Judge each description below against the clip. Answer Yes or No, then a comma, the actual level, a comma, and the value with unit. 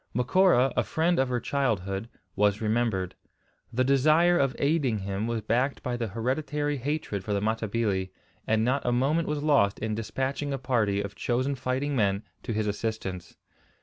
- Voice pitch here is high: No, low, 120 Hz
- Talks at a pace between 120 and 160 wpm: No, average, 170 wpm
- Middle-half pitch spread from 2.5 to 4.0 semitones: No, average, 4.7 semitones